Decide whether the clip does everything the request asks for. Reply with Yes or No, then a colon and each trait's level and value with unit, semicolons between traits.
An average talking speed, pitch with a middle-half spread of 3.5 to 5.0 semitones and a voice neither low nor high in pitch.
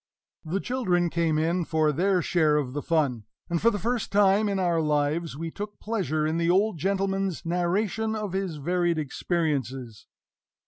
Yes: average, 170 wpm; average, 4.0 semitones; medium, 175 Hz